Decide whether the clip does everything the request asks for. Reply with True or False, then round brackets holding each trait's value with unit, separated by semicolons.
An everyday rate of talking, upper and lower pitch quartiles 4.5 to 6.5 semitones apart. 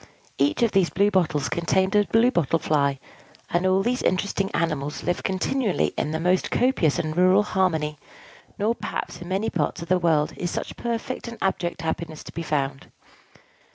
False (185 wpm; 4.0 semitones)